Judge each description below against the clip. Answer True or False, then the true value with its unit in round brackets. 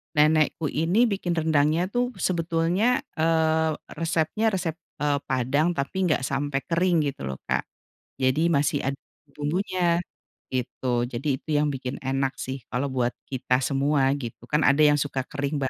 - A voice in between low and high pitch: True (150 Hz)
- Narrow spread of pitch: False (3.5 semitones)